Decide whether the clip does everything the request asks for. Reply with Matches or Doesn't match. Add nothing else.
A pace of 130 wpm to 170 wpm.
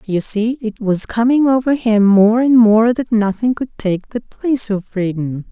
Doesn't match